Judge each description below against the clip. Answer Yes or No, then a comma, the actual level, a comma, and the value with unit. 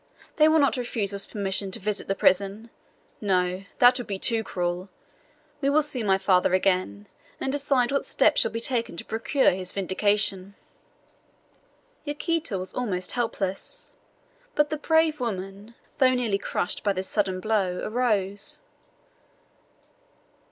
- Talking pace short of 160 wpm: Yes, average, 145 wpm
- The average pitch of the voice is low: No, high, 205 Hz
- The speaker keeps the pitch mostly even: No, average, 4.7 semitones